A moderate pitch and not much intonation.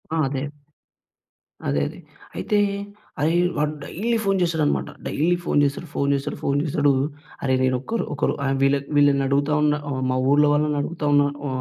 Yes: medium, 145 Hz; narrow, 1.9 semitones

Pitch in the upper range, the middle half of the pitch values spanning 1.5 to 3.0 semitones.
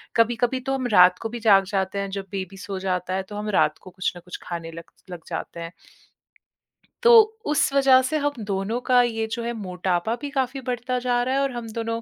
No: high, 225 Hz; average, 4.9 semitones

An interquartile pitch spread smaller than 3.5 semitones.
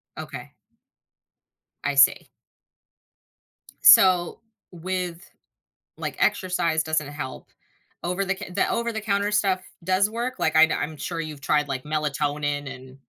No: average, 4.2 semitones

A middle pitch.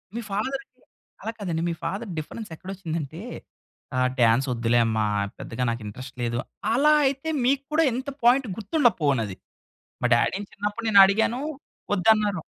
No: high, 195 Hz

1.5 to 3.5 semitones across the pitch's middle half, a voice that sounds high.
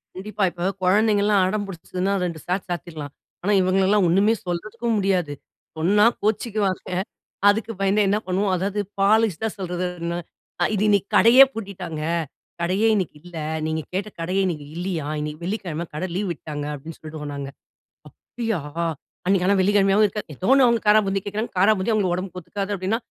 Yes: average, 3.1 semitones; high, 195 Hz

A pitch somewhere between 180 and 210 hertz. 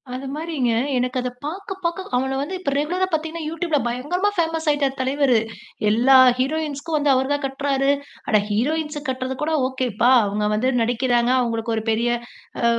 No: very high, 270 Hz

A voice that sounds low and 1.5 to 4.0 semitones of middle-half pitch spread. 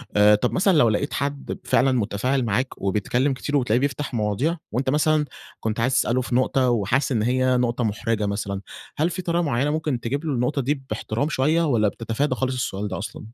No: low, 125 Hz; average, 4.5 semitones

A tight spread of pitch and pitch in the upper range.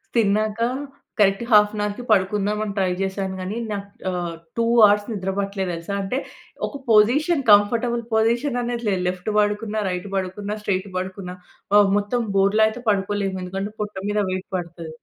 Yes: narrow, 2.1 semitones; high, 205 Hz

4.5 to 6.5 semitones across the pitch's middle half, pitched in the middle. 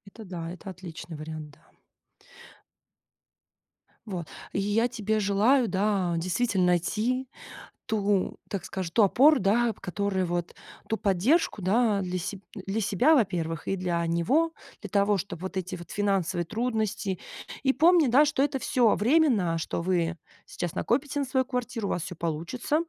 No: average, 5.2 semitones; high, 200 Hz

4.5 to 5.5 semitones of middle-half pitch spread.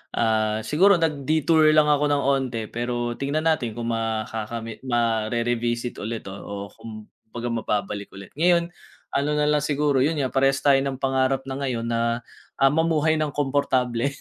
No: average, 4.1 semitones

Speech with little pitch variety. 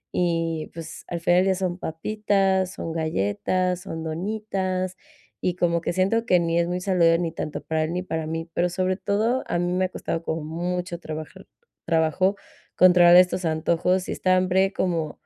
Yes: narrow, 2.1 semitones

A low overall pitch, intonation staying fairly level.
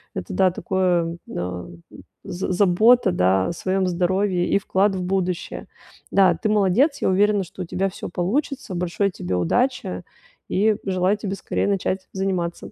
No: medium, 185 Hz; narrow, 2.2 semitones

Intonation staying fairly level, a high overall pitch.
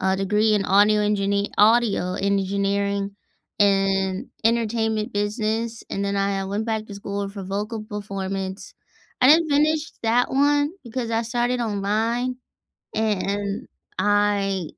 Yes: narrow, 2.3 semitones; high, 205 Hz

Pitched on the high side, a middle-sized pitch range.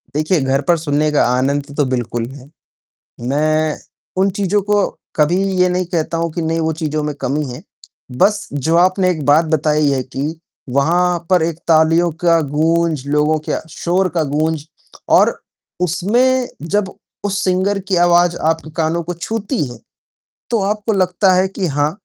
No: medium, 165 Hz; average, 3.5 semitones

